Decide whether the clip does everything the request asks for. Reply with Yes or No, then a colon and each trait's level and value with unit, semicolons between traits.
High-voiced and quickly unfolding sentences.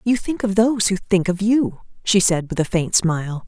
Yes: high, 195 Hz; fast, 240 wpm